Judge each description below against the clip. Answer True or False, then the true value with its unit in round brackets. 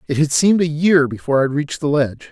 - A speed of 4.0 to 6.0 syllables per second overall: False (6.5 syllables/s)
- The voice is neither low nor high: True (150 Hz)